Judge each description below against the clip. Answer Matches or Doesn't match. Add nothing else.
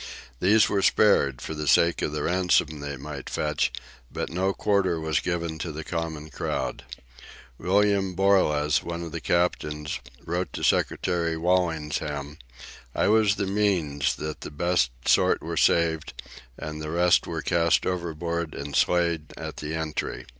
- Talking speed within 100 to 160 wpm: Matches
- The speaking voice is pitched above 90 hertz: Doesn't match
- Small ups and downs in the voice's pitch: Doesn't match